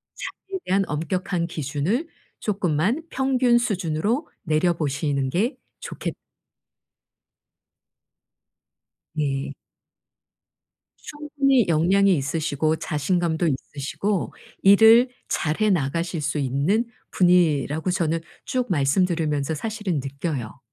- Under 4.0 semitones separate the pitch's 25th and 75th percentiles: No, wide, 5.5 semitones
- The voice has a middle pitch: Yes, medium, 170 Hz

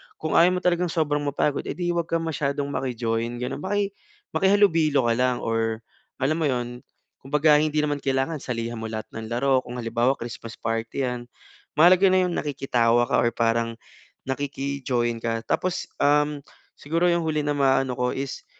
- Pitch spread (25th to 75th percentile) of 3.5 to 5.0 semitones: Yes, average, 4.5 semitones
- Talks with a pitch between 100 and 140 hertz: Yes, low, 135 Hz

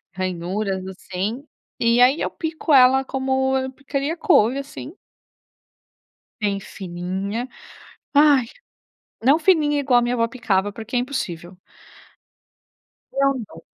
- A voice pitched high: Yes, high, 245 Hz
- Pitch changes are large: Yes, wide, 5.8 semitones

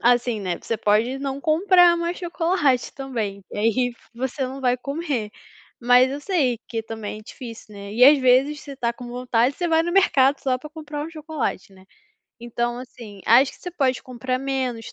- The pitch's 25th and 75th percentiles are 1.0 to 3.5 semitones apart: No, average, 3.9 semitones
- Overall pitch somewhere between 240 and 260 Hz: Yes, very high, 255 Hz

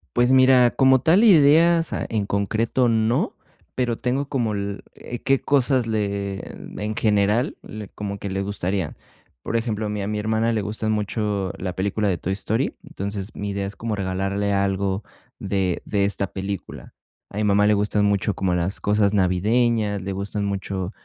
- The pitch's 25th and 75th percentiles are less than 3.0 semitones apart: Yes, narrow, 2.6 semitones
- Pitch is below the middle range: Yes, low, 105 Hz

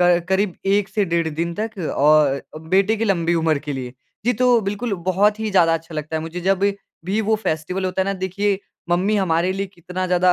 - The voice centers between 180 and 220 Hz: Yes, medium, 185 Hz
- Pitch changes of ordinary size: Yes, average, 3.3 semitones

